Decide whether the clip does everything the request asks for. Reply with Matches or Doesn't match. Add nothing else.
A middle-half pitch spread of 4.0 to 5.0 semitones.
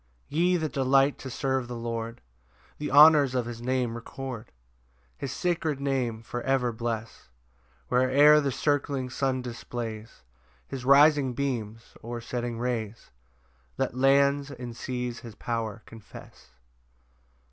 Doesn't match